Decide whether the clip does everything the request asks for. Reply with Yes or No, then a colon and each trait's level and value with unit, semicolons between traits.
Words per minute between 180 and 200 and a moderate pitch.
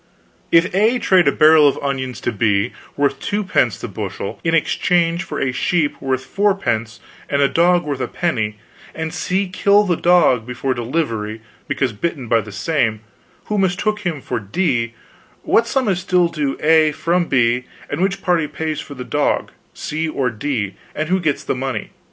Yes: average, 185 wpm; medium, 150 Hz